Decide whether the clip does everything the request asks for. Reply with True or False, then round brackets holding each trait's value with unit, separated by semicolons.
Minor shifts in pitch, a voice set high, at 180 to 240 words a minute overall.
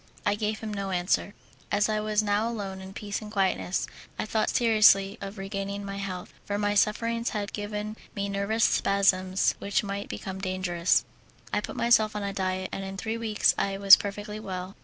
True (1.6 semitones; 200 Hz; 185 wpm)